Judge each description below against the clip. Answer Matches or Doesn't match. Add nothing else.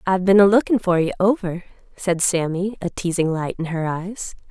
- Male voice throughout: Doesn't match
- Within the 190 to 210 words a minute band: Matches